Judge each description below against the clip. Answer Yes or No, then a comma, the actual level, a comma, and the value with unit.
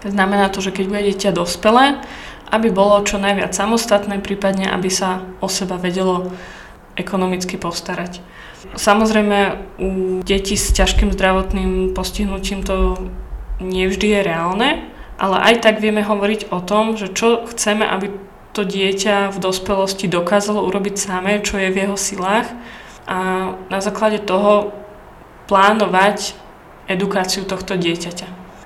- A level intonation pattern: Yes, narrow, 1.6 semitones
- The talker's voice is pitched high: Yes, high, 195 Hz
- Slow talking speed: No, average, 130 wpm